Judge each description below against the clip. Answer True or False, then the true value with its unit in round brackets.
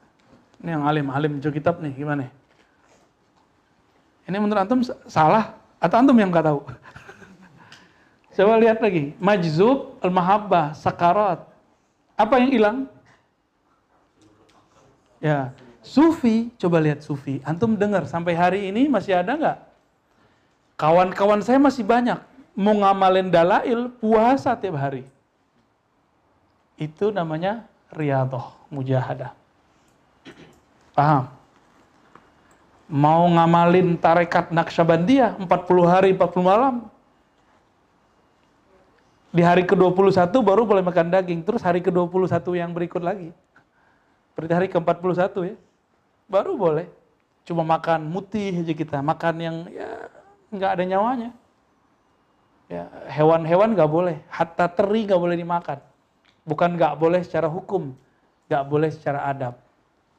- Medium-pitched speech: True (175 Hz)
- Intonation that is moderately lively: True (4.4 semitones)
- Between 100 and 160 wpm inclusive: True (110 wpm)